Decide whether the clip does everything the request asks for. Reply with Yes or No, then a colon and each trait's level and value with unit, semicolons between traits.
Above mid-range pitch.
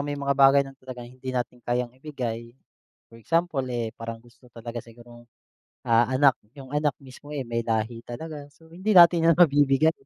No: low, 130 Hz